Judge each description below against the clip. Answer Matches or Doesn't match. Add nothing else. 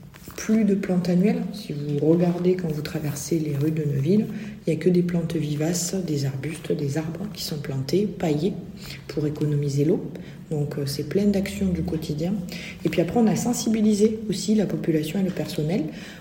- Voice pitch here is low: Doesn't match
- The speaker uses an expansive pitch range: Doesn't match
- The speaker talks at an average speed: Matches